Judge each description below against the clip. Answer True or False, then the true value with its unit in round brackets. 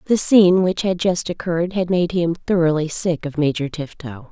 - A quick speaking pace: False (195 wpm)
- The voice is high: False (170 Hz)